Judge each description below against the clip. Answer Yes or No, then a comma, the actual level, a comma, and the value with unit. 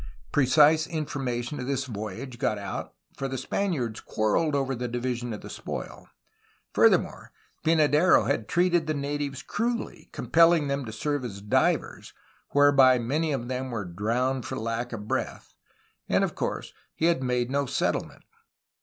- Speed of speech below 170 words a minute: Yes, average, 160 wpm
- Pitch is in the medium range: No, low, 130 Hz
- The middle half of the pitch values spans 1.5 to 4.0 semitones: Yes, average, 3.7 semitones